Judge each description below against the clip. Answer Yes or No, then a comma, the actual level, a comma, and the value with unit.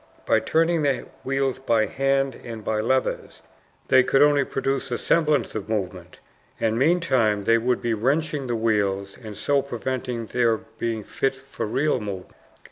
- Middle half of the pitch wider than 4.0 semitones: No, average, 3.7 semitones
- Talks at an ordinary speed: Yes, average, 160 wpm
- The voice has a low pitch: Yes, low, 125 Hz